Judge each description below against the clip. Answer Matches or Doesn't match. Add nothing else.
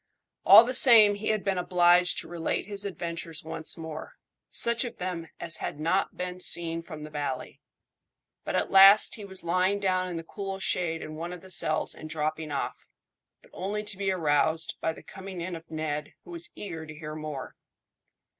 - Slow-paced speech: Doesn't match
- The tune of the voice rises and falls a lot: Doesn't match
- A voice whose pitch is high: Doesn't match